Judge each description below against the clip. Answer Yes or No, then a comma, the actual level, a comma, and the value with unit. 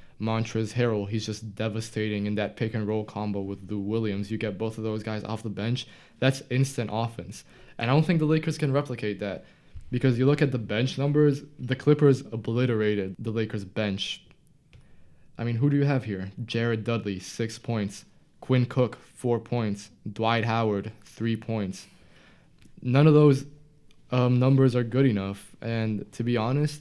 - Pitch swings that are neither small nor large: Yes, average, 3.4 semitones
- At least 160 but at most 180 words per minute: Yes, average, 175 wpm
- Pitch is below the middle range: Yes, low, 115 Hz